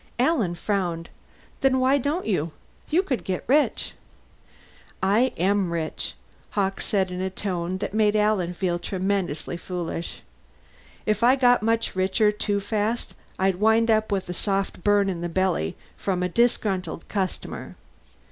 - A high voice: Yes, high, 195 Hz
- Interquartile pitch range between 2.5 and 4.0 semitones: Yes, average, 3.5 semitones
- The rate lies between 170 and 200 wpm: No, average, 145 wpm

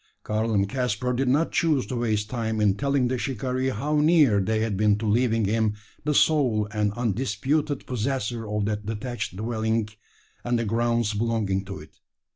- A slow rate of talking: No, average, 175 wpm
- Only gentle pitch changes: No, average, 3.3 semitones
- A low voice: Yes, low, 115 Hz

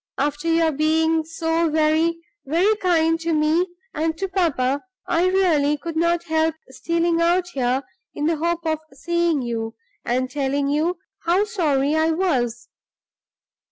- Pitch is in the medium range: No, very high, 320 Hz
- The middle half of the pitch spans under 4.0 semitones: Yes, average, 2.7 semitones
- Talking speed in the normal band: Yes, average, 145 wpm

